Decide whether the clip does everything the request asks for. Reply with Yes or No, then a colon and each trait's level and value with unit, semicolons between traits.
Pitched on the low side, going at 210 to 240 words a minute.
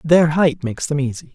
No: medium, 150 Hz; fast, 225 wpm